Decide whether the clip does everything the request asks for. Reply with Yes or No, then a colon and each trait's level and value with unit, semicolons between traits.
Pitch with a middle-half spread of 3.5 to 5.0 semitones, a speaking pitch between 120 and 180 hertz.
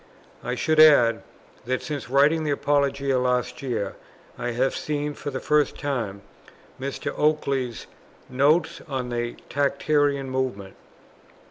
No: average, 2.7 semitones; low, 135 Hz